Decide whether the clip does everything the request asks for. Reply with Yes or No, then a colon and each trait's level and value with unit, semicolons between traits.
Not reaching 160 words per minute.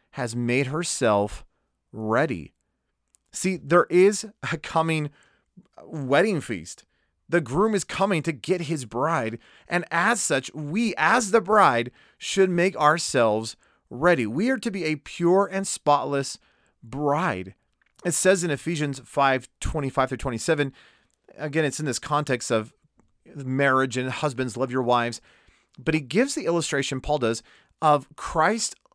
Yes: average, 140 wpm